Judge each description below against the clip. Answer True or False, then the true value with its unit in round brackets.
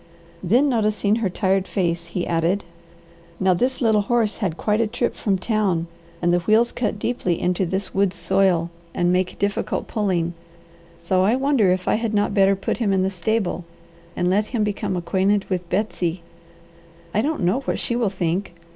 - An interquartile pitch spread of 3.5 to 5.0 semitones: False (3.1 semitones)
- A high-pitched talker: True (195 Hz)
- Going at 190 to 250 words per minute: False (180 wpm)